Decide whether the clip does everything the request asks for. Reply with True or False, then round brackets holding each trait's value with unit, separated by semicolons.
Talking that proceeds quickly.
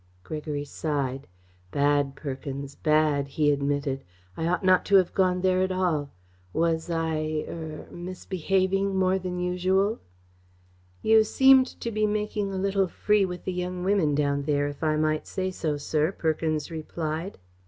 False (155 wpm)